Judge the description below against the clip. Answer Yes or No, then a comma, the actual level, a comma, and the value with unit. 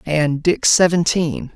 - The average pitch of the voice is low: No, medium, 165 Hz